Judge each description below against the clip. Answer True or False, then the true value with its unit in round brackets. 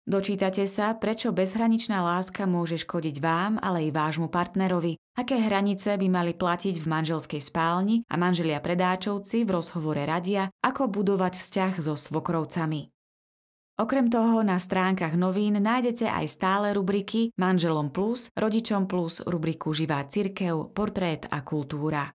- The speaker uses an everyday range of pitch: True (3.9 semitones)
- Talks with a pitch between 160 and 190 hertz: True (185 Hz)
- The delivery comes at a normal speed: True (135 wpm)